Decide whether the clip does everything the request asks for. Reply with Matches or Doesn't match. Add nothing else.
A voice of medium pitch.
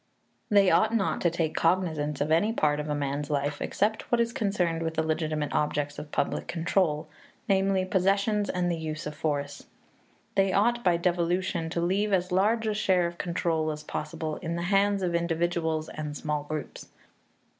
Matches